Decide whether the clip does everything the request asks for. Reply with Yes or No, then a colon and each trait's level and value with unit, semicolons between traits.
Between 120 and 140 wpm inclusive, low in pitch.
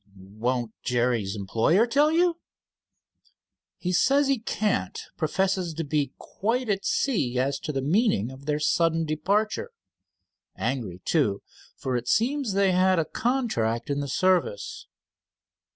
No: slow, 135 wpm; medium, 165 Hz